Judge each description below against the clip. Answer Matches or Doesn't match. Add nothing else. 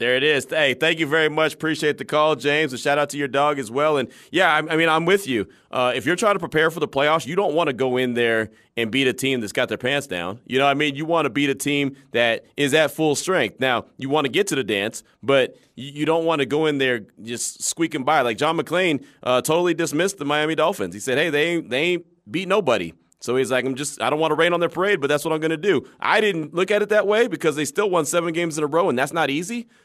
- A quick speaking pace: Matches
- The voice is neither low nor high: Matches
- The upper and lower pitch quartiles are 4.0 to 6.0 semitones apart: Doesn't match